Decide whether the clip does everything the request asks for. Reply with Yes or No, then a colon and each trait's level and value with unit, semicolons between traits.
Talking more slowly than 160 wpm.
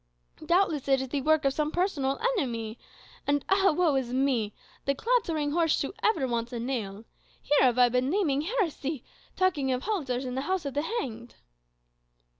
No: average, 180 wpm